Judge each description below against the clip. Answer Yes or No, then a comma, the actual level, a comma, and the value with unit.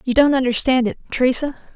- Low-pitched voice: No, very high, 260 Hz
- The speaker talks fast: No, average, 170 wpm